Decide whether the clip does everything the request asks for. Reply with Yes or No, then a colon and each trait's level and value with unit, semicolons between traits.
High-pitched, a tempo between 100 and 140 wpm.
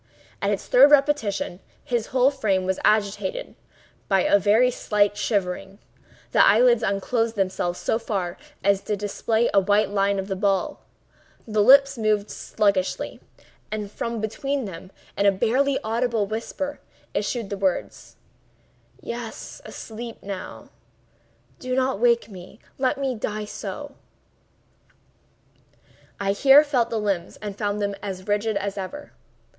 Yes: high, 210 Hz; slow, 135 wpm